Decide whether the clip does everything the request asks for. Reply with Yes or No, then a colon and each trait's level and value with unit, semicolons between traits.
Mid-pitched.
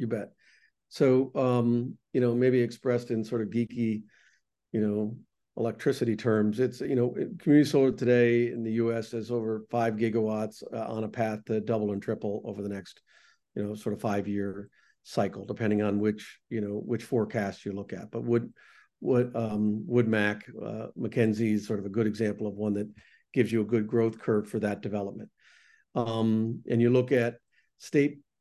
No: low, 115 Hz